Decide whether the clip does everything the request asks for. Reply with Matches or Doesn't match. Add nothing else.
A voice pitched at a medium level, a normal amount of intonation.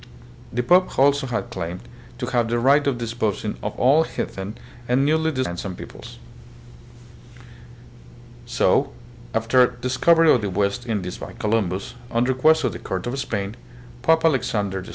Doesn't match